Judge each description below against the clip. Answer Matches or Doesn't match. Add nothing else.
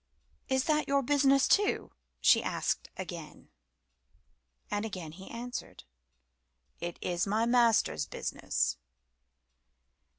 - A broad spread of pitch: Matches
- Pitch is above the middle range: Matches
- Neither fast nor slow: Doesn't match